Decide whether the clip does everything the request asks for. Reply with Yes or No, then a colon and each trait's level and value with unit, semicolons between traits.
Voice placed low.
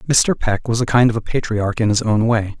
Yes: low, 115 Hz